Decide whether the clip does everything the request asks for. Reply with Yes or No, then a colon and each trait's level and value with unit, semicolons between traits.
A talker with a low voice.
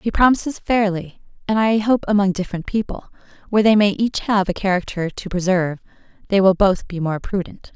No: high, 200 Hz